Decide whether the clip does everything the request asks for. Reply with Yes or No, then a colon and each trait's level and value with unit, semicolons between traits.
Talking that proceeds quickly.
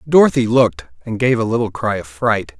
Yes: fast, 210 wpm